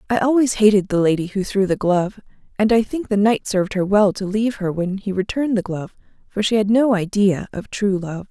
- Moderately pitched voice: No, high, 205 Hz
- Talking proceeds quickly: Yes, fast, 240 wpm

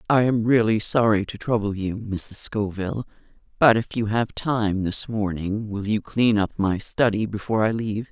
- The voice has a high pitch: No, low, 110 Hz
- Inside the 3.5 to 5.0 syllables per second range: Yes, 4.8 syllables/s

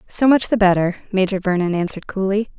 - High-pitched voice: Yes, high, 195 Hz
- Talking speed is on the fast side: No, average, 185 wpm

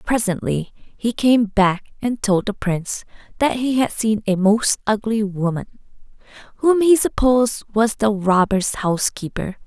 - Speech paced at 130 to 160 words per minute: Yes, average, 145 wpm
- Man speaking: No, female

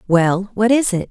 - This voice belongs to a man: No, female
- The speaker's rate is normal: Yes, average, 165 wpm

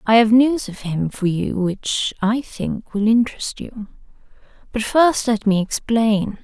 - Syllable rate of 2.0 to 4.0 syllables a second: Yes, 3.9 syllables/s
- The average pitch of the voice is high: Yes, high, 220 Hz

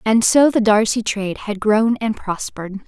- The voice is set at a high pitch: Yes, high, 215 Hz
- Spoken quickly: No, average, 190 wpm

